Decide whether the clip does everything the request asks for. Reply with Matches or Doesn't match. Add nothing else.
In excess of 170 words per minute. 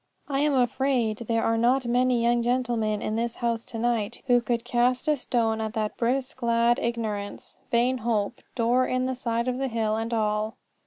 Matches